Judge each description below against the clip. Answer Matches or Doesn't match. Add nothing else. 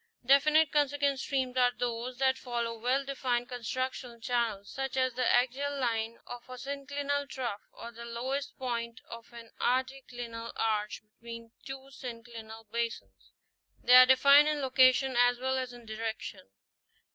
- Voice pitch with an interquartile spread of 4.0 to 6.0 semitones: Doesn't match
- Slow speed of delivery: Doesn't match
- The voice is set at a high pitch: Matches